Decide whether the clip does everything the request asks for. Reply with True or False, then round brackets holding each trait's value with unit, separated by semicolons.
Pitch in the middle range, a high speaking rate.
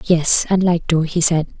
True (165 Hz; 225 wpm)